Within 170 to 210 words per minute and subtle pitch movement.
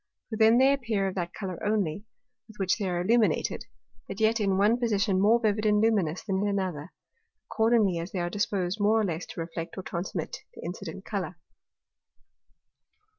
No: average, 180 wpm; average, 3.2 semitones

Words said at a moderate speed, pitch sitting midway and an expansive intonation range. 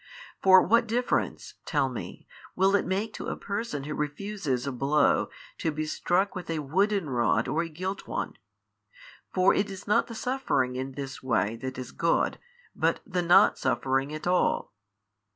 Yes: average, 170 wpm; medium, 165 Hz; wide, 6.4 semitones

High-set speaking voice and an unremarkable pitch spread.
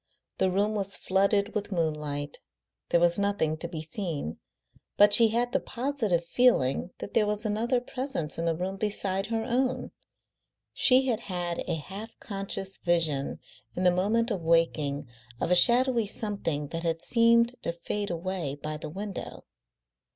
Yes: high, 195 Hz; average, 5.0 semitones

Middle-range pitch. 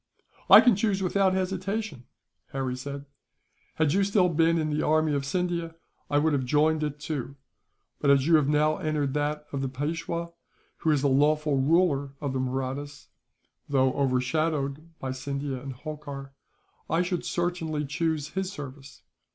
Yes: medium, 150 Hz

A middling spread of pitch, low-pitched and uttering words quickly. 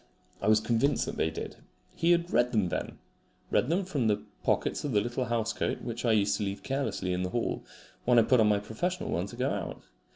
Yes: average, 4.2 semitones; low, 115 Hz; fast, 235 wpm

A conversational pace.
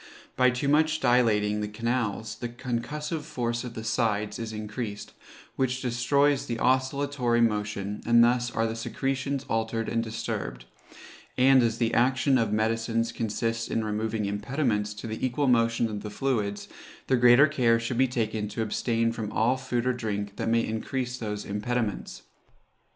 Yes: average, 160 wpm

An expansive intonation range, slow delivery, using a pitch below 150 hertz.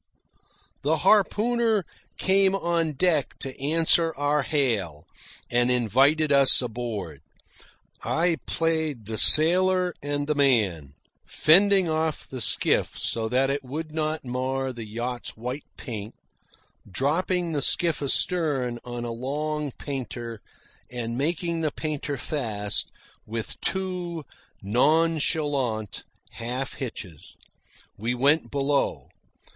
No: average, 5.0 semitones; slow, 110 wpm; medium, 140 Hz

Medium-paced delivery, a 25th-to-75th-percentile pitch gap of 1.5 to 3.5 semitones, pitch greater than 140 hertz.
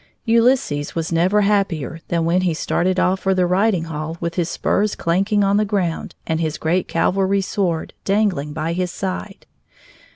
Yes: average, 170 wpm; average, 3.2 semitones; medium, 185 Hz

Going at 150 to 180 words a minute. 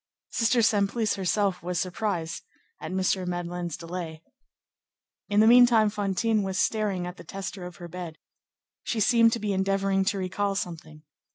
Yes: average, 155 wpm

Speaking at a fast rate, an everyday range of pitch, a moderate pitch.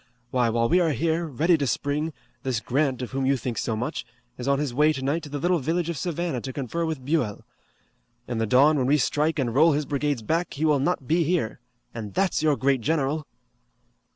Yes: fast, 220 wpm; average, 3.9 semitones; medium, 145 Hz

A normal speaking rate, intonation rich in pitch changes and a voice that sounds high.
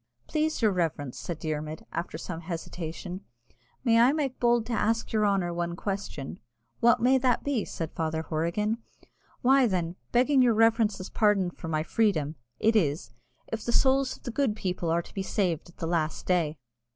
Yes: average, 180 wpm; wide, 5.9 semitones; high, 195 Hz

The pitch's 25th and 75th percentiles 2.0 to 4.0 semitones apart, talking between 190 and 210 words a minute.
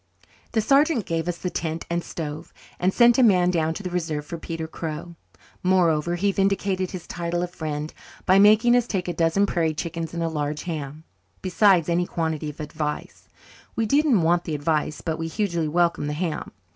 Yes: average, 2.9 semitones; average, 195 wpm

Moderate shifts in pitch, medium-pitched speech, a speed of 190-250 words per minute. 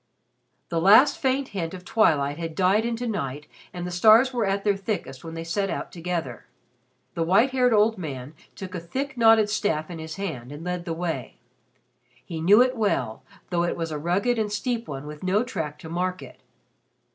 Yes: average, 5.0 semitones; medium, 180 Hz; average, 200 wpm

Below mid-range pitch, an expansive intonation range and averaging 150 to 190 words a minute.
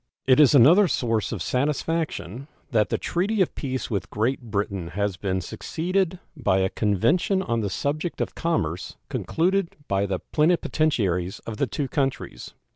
Yes: low, 130 Hz; wide, 8.3 semitones; average, 155 wpm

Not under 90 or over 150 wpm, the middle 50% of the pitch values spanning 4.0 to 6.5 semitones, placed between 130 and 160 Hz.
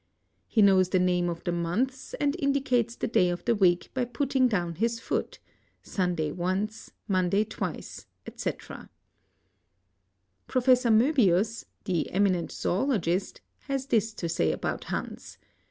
No: average, 140 wpm; wide, 5.6 semitones; high, 205 Hz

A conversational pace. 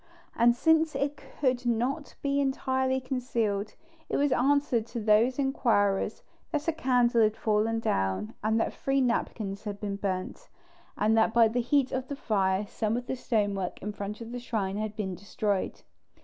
Yes: average, 175 wpm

